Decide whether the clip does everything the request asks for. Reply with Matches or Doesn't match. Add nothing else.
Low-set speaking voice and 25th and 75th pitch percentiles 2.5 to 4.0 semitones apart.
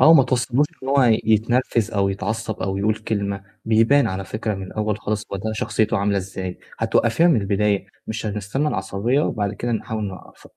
Matches